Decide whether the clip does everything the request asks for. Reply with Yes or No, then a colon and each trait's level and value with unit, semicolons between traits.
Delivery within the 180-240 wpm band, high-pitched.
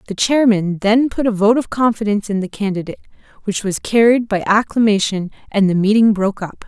Yes: average, 190 wpm; high, 210 Hz